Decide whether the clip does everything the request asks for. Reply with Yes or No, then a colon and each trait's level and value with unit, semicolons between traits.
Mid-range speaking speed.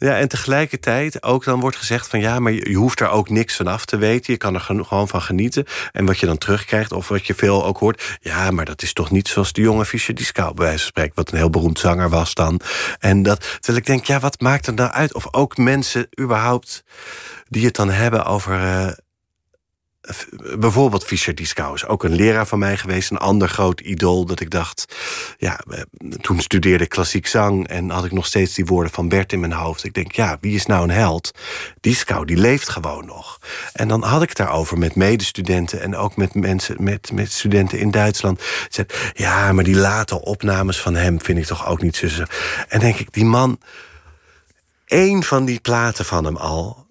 No: fast, 215 wpm